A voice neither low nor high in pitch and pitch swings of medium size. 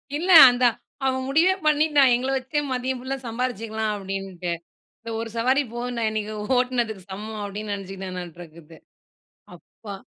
No: high, 230 Hz; average, 4.8 semitones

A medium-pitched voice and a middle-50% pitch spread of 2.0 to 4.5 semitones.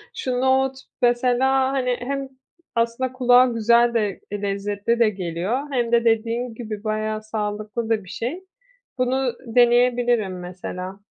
No: high, 235 Hz; average, 2.8 semitones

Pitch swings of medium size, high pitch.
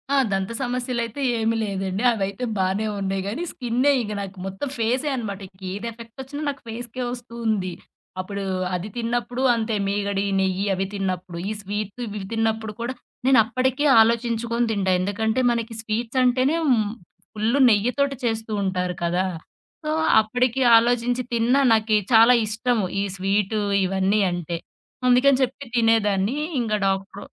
Yes: average, 3.6 semitones; high, 220 Hz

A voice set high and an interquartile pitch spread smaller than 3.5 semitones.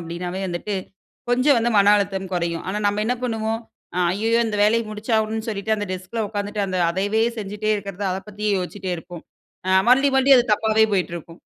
Yes: high, 205 Hz; average, 2.8 semitones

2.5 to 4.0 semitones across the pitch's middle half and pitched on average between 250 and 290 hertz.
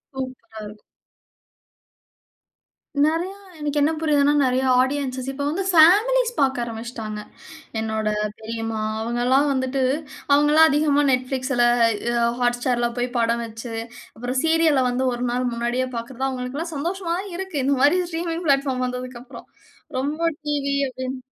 Yes: average, 3.4 semitones; very high, 260 Hz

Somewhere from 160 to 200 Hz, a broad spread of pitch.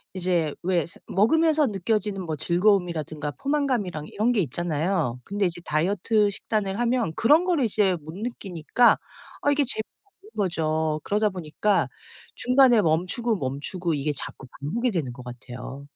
Yes: high, 190 Hz; wide, 6.5 semitones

